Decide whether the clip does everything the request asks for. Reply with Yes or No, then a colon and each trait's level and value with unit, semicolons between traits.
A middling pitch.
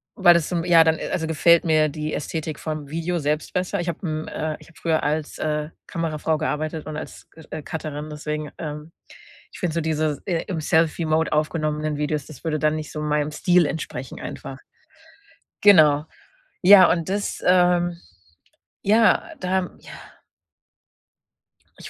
Yes: medium, 155 Hz